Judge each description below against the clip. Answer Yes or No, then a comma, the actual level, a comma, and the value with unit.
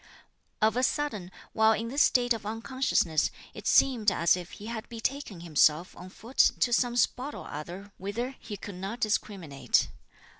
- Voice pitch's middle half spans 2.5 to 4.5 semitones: No, average, 4.9 semitones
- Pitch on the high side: Yes, high, 220 Hz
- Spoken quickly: No, average, 165 wpm